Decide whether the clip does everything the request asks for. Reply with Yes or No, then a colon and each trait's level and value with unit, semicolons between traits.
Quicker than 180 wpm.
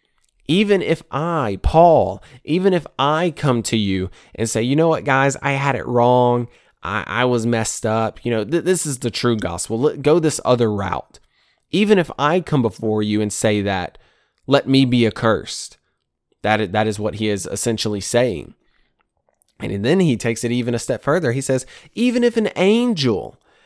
Yes: average, 190 wpm